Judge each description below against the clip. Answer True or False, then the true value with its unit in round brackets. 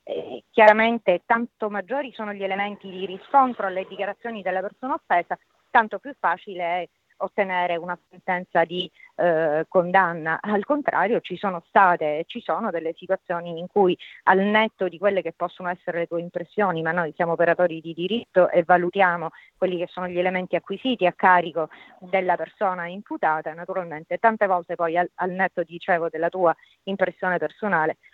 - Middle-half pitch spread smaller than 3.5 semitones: True (2.6 semitones)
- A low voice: False (180 Hz)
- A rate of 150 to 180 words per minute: True (165 wpm)